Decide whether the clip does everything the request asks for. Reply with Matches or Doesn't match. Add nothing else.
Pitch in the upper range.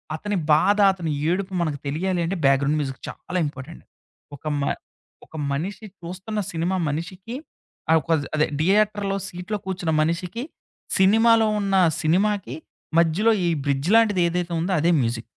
Doesn't match